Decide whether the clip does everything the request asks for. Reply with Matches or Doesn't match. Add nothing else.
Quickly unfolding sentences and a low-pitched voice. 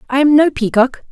Doesn't match